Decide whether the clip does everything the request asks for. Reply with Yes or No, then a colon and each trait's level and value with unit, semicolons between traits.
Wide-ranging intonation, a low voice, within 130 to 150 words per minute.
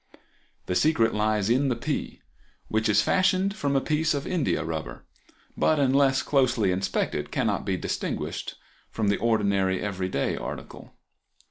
Yes: wide, 5.9 semitones; low, 115 Hz; average, 140 wpm